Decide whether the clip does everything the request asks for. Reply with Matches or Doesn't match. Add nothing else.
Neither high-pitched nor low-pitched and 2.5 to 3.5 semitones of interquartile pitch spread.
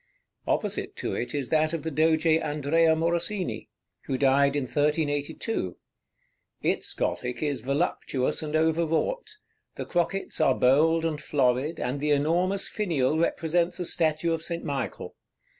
Matches